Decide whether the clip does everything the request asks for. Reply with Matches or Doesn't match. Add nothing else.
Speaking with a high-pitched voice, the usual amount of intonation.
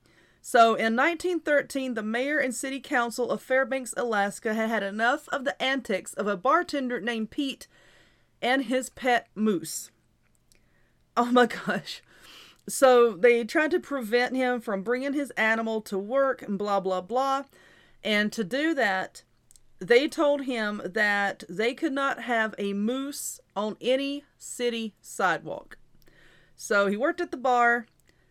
Matches